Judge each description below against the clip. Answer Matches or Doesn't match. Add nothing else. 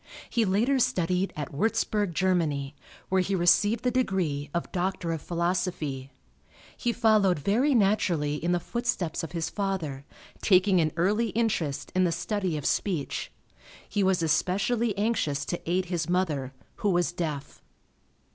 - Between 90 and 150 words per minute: Matches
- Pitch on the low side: Doesn't match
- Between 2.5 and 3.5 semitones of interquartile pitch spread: Doesn't match